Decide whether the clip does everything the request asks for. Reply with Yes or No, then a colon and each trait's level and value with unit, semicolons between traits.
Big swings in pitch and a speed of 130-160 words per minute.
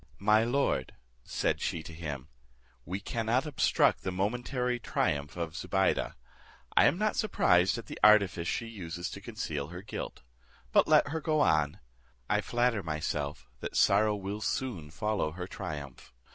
Yes: wide, 6.6 semitones; average, 155 wpm